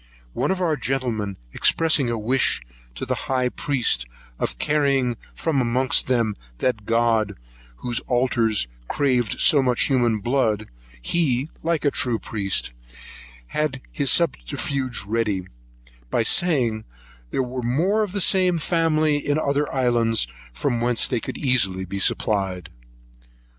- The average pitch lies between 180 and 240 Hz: No, low, 125 Hz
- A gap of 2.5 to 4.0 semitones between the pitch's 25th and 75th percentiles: No, average, 4.4 semitones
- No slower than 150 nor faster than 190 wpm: No, slow, 135 wpm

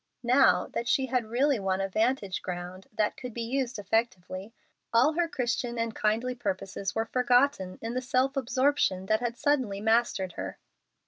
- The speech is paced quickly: No, average, 170 wpm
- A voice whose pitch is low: No, high, 230 Hz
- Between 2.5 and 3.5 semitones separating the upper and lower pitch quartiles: No, average, 4.4 semitones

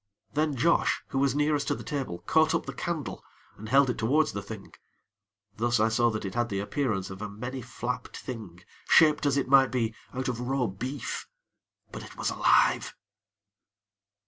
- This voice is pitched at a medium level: No, low, 125 Hz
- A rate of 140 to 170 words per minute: No, average, 185 wpm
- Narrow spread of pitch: No, average, 4.1 semitones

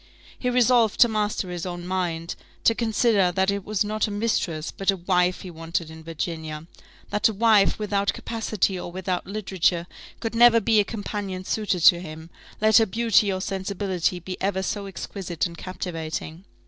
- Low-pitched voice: No, high, 190 Hz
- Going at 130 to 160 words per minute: No, average, 175 wpm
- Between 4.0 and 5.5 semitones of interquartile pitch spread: No, average, 3.3 semitones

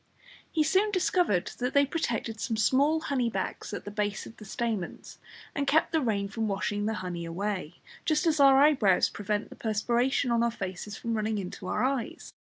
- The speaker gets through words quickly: No, average, 195 wpm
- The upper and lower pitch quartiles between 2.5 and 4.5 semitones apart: No, average, 5.2 semitones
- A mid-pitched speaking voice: No, high, 225 Hz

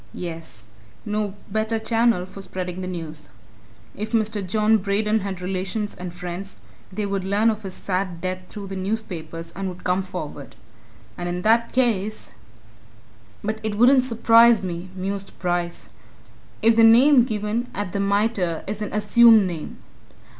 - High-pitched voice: Yes, high, 200 Hz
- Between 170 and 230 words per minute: No, average, 155 wpm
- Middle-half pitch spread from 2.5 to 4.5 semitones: Yes, average, 3.2 semitones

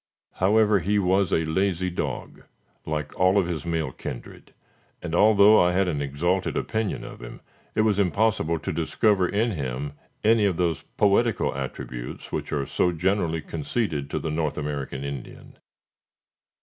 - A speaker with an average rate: Yes, average, 155 wpm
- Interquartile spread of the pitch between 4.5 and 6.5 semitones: Yes, average, 4.9 semitones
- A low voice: Yes, very low, 90 Hz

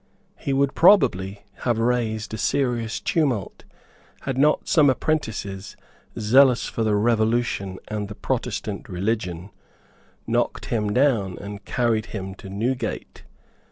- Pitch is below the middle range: Yes, low, 110 Hz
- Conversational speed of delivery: No, slow, 125 wpm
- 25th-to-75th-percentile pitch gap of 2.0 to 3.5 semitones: No, average, 3.9 semitones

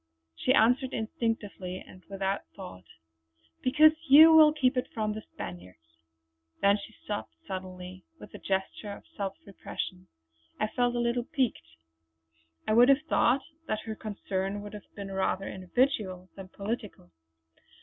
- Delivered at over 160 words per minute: No, average, 145 wpm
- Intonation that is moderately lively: Yes, average, 4.4 semitones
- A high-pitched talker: Yes, high, 205 Hz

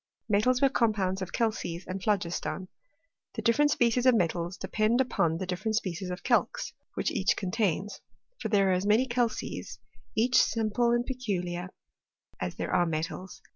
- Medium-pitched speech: No, high, 205 Hz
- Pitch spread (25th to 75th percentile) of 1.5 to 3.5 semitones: No, average, 4.6 semitones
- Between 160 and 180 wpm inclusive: Yes, average, 165 wpm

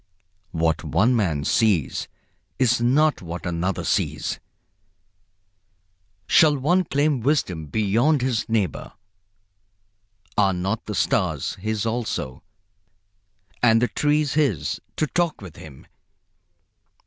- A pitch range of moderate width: No, wide, 7.6 semitones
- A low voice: Yes, low, 115 Hz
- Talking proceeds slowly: Yes, slow, 105 wpm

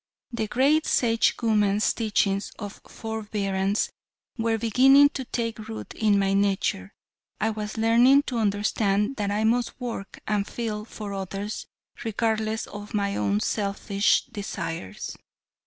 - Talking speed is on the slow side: Yes, slow, 125 wpm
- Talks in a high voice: Yes, high, 215 Hz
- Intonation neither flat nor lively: No, narrow, 2.3 semitones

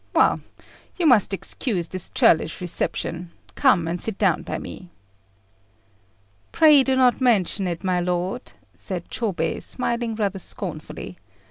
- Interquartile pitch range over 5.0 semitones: Yes, wide, 5.5 semitones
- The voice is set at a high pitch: Yes, high, 195 Hz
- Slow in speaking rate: Yes, slow, 130 wpm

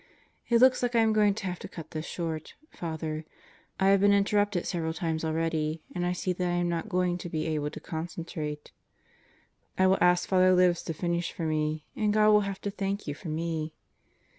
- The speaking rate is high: Yes, fast, 215 wpm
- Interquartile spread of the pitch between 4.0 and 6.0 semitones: No, average, 3.6 semitones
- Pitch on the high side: No, medium, 175 Hz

